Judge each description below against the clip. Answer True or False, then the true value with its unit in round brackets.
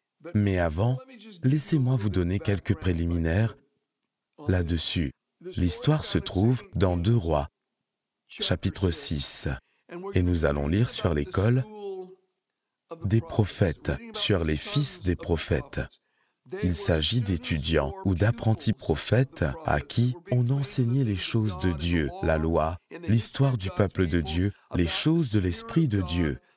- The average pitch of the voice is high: False (100 Hz)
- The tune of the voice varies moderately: False (6.3 semitones)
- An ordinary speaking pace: False (125 wpm)